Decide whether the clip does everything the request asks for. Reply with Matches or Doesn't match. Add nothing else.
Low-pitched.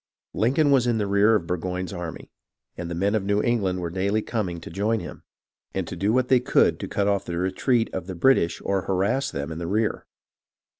Matches